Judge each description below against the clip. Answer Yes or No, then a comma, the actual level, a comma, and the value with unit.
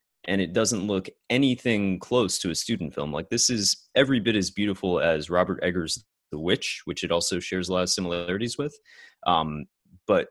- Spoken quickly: No, average, 190 wpm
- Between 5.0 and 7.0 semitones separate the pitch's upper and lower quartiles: Yes, wide, 5.5 semitones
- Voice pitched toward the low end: Yes, low, 100 Hz